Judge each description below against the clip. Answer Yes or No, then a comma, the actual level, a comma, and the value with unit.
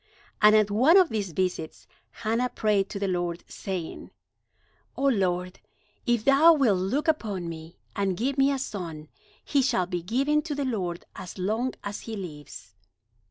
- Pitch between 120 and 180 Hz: No, high, 205 Hz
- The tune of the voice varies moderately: No, wide, 6.3 semitones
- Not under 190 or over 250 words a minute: No, average, 165 wpm